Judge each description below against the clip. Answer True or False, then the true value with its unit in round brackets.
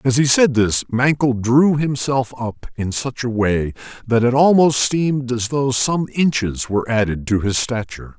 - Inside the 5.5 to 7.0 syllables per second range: False (4.5 syllables/s)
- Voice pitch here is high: False (125 Hz)